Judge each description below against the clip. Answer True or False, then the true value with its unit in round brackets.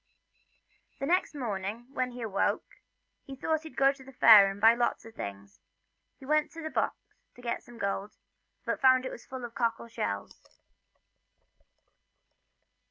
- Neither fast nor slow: True (170 wpm)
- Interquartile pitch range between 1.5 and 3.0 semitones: False (4.4 semitones)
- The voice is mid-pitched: False (240 Hz)